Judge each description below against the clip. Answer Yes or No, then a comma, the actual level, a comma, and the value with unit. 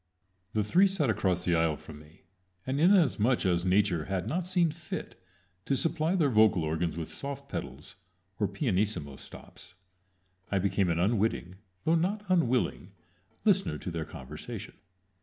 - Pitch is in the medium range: No, low, 105 Hz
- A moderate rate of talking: Yes, average, 150 wpm